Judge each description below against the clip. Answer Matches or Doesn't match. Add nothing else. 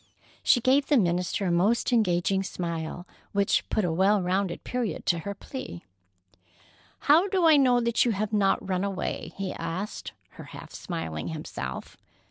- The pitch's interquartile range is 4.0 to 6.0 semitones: Matches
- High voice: Matches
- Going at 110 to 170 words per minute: Matches